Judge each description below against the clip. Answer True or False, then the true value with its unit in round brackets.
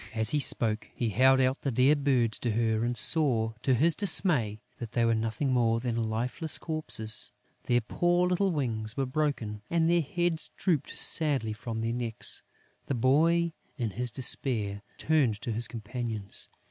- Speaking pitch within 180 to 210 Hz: False (125 Hz)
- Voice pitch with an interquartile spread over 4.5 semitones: True (5.0 semitones)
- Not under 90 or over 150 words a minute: False (170 wpm)